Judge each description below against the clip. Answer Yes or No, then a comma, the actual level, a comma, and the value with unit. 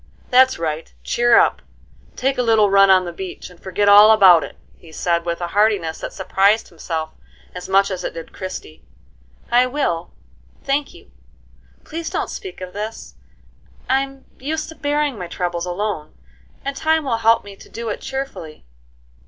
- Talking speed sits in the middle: Yes, average, 170 wpm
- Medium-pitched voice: No, high, 205 Hz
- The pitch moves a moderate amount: No, wide, 6.5 semitones